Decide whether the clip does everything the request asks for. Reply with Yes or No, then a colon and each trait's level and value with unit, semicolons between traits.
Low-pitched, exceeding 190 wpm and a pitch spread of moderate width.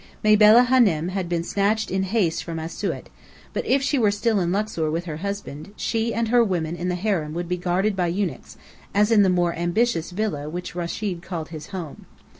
No: medium, 185 Hz; fast, 205 wpm; average, 3.9 semitones